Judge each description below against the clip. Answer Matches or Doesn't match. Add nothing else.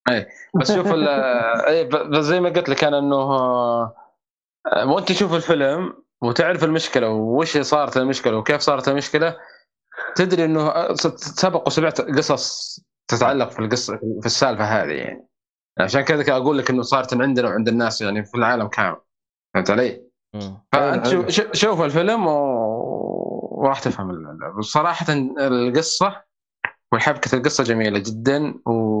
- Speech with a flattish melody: Doesn't match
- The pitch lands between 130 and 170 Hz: Matches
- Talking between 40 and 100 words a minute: Doesn't match